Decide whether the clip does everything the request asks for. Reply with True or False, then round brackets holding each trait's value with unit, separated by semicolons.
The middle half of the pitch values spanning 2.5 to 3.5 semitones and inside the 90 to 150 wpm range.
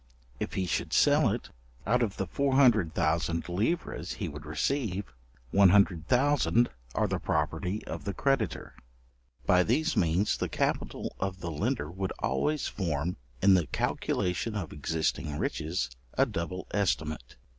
False (5.1 semitones; 135 wpm)